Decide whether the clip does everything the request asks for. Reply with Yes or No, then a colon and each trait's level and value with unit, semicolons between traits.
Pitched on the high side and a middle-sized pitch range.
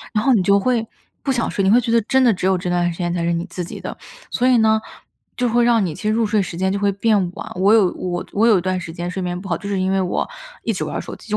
Yes: high, 200 Hz; average, 4.0 semitones